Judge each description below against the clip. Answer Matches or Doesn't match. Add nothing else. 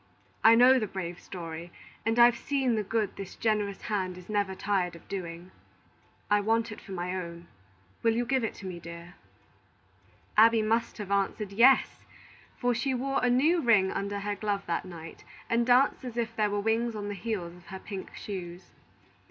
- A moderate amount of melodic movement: Matches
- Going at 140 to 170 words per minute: Doesn't match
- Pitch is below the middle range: Doesn't match